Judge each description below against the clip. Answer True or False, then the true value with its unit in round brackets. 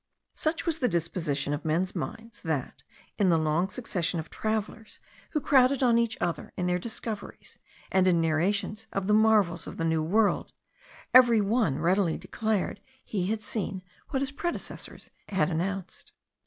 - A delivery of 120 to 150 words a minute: False (160 wpm)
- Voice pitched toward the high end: True (195 Hz)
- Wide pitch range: False (4.9 semitones)